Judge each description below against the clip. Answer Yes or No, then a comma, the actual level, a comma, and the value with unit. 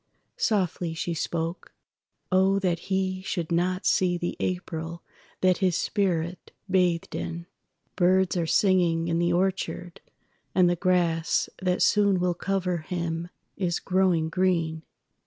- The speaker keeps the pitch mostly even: Yes, narrow, 1.8 semitones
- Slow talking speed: Yes, slow, 120 wpm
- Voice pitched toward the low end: No, medium, 180 Hz